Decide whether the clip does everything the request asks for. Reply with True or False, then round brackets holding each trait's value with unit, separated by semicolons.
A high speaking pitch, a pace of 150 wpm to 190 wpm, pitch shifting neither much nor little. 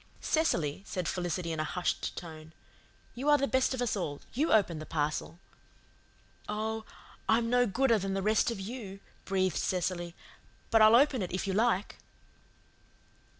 True (195 Hz; 160 wpm; 5.0 semitones)